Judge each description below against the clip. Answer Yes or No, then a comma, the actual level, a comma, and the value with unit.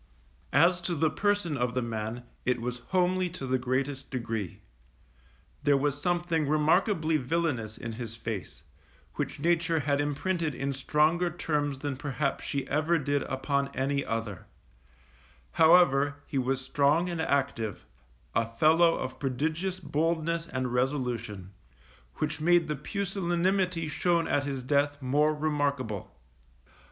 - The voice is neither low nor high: Yes, medium, 145 Hz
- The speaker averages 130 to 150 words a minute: Yes, slow, 135 wpm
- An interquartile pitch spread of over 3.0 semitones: Yes, average, 4.3 semitones